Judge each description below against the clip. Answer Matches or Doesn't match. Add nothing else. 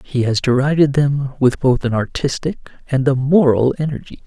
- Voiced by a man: Matches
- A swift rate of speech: Doesn't match